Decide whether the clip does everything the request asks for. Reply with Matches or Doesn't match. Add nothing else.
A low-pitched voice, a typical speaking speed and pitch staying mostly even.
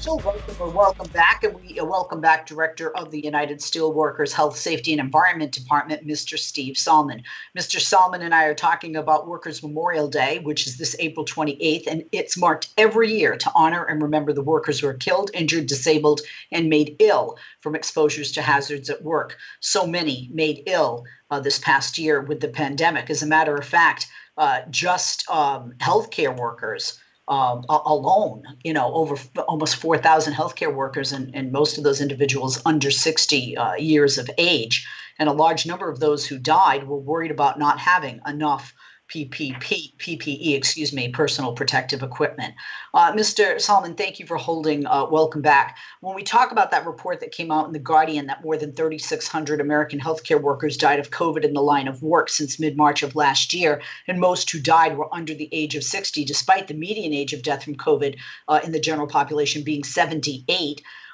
Doesn't match